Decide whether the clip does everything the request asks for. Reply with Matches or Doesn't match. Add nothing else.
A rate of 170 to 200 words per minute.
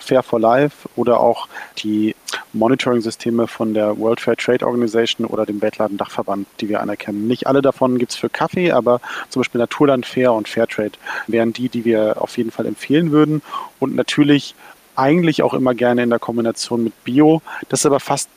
Matches